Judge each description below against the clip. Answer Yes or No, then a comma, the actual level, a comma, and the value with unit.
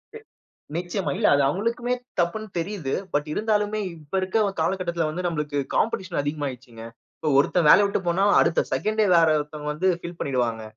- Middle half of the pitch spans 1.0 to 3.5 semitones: No, average, 5.3 semitones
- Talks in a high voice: No, medium, 170 Hz